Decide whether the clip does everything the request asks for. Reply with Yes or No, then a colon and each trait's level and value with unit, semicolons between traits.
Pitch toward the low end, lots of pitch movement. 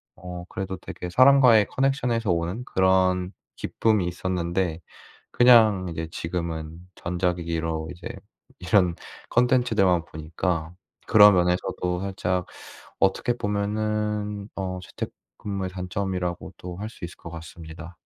No: very low, 90 Hz; average, 3.1 semitones